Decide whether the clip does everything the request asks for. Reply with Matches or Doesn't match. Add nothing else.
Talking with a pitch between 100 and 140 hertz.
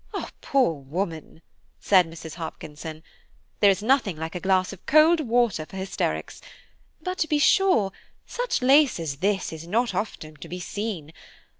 Doesn't match